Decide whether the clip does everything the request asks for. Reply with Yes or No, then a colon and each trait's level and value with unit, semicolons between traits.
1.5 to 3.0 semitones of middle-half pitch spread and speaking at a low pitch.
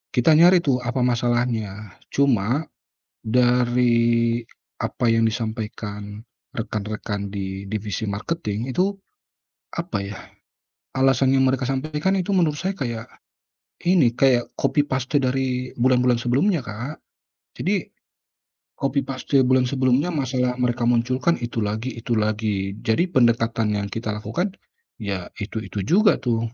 No: average, 3.5 semitones; low, 125 Hz